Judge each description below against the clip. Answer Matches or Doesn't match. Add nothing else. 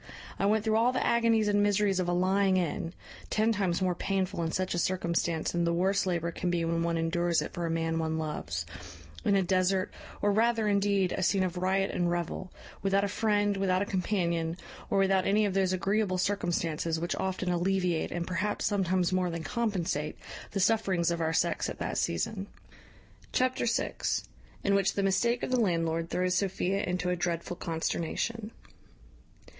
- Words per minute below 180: Doesn't match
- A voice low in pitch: Doesn't match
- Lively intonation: Doesn't match